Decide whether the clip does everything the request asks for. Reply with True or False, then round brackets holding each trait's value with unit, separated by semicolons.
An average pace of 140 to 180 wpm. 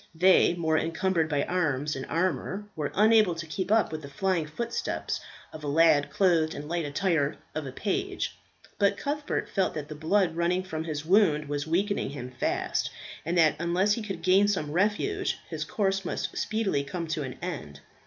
False (190 wpm)